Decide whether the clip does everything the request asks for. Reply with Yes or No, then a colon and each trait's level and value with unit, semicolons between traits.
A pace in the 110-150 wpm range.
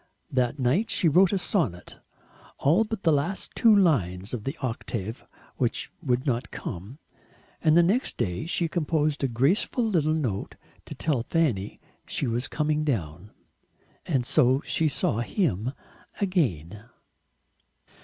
Yes: average, 140 wpm